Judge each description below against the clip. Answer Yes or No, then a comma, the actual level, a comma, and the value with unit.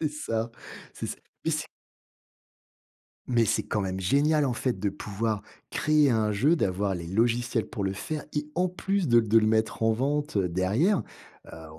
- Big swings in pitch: Yes, wide, 6.6 semitones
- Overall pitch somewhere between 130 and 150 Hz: No, low, 115 Hz